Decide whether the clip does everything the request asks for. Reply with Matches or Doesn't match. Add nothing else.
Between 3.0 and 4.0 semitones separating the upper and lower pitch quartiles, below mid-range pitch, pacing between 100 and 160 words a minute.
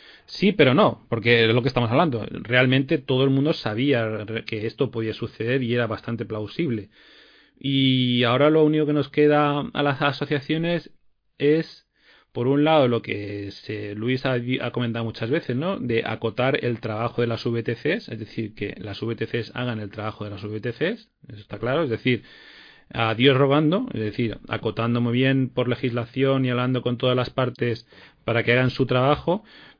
Doesn't match